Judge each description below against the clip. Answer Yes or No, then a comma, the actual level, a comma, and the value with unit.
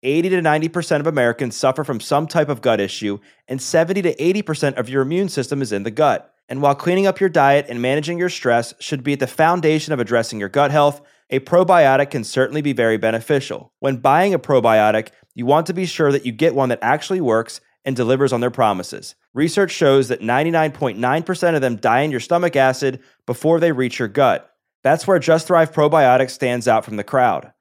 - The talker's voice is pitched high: No, medium, 140 Hz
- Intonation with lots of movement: No, average, 4.5 semitones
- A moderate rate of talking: No, fast, 215 wpm